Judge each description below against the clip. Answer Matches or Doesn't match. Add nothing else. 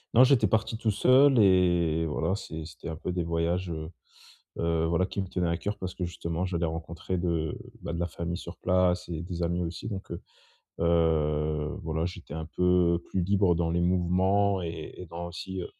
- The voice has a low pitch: Matches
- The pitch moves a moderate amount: Doesn't match